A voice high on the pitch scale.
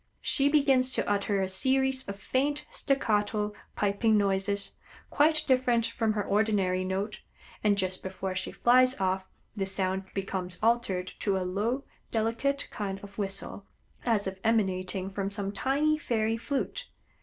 Yes: high, 205 Hz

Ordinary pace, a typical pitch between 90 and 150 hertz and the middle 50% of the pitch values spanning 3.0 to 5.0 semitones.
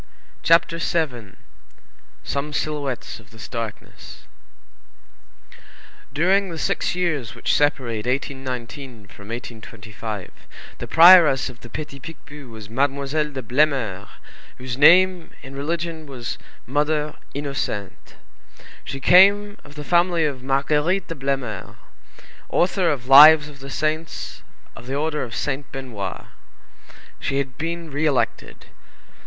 No: slow, 120 wpm; medium, 140 Hz; average, 4.3 semitones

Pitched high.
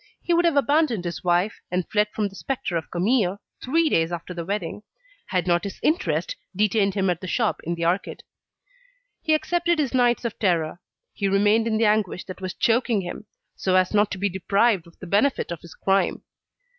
Yes: high, 200 Hz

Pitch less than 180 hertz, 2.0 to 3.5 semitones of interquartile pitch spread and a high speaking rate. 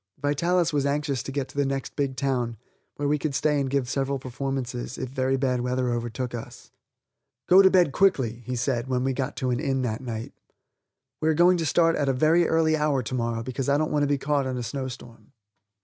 Yes: low, 135 Hz; average, 2.7 semitones; fast, 225 wpm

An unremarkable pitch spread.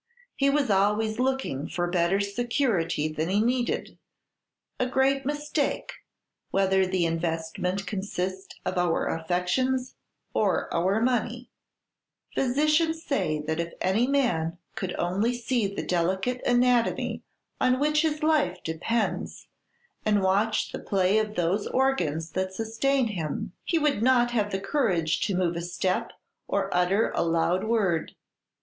No: wide, 6.0 semitones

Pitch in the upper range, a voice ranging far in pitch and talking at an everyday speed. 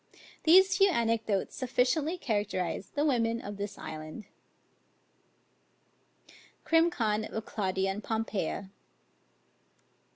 No: high, 225 Hz; wide, 6.1 semitones; slow, 95 wpm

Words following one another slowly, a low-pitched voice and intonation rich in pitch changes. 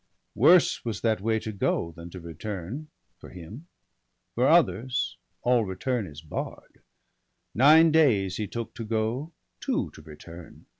No: average, 150 wpm; low, 110 Hz; wide, 5.8 semitones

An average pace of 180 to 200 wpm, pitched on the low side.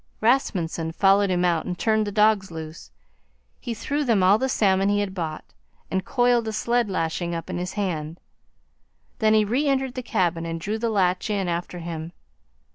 No: average, 190 wpm; high, 195 Hz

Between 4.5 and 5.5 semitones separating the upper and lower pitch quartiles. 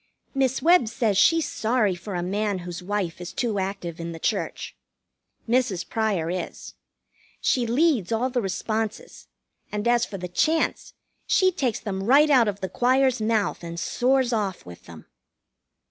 Yes: average, 5.2 semitones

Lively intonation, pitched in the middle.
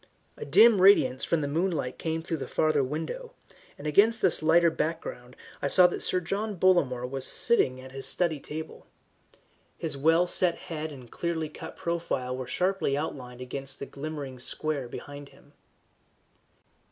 No: average, 4.2 semitones; medium, 155 Hz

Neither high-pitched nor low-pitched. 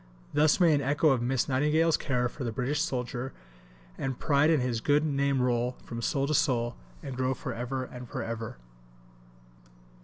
No: low, 130 Hz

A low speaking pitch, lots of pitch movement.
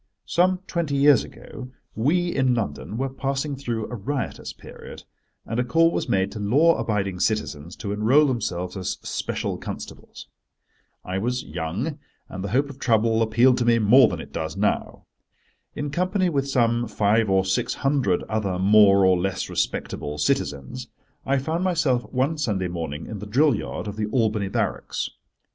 Yes: low, 115 Hz; wide, 6.0 semitones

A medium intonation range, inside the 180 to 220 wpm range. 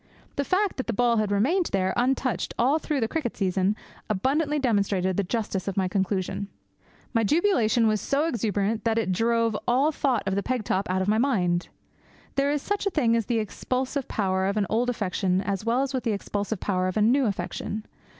Yes: average, 4.8 semitones; fast, 205 wpm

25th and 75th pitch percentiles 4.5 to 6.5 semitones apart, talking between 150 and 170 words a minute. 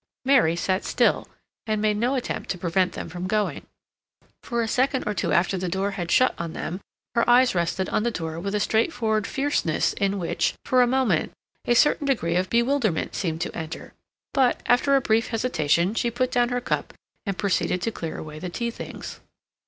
No: wide, 5.5 semitones; average, 200 wpm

